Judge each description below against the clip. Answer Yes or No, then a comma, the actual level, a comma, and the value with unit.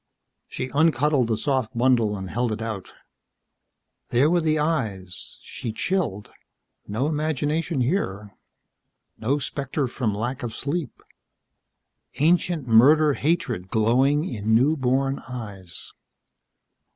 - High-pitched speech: No, low, 130 Hz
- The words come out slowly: Yes, slow, 110 wpm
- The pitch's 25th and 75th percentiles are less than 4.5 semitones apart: No, average, 5.2 semitones